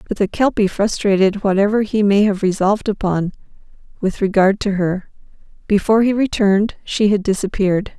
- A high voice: Yes, high, 200 Hz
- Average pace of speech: Yes, average, 150 wpm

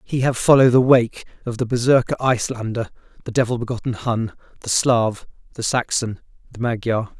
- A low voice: Yes, low, 120 Hz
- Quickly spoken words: No, average, 160 wpm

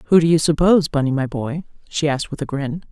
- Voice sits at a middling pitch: Yes, medium, 150 Hz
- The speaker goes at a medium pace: No, fast, 245 wpm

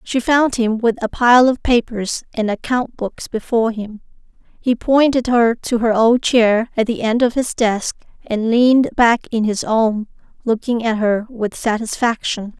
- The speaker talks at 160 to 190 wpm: Yes, average, 170 wpm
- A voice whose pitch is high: Yes, high, 230 Hz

